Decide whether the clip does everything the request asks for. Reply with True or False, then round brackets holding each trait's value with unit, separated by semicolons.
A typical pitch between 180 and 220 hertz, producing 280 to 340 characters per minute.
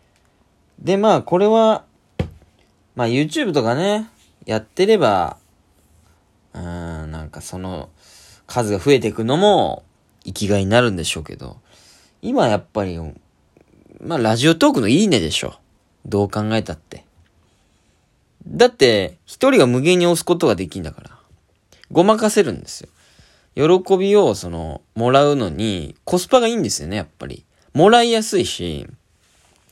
False (110 Hz; 290 characters per minute)